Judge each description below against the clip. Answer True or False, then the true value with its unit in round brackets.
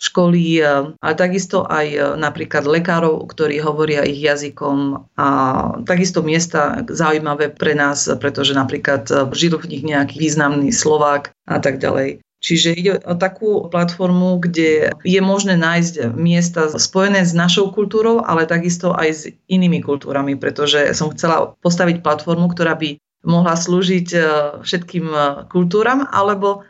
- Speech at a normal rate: True (135 wpm)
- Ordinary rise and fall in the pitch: True (3.6 semitones)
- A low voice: False (165 Hz)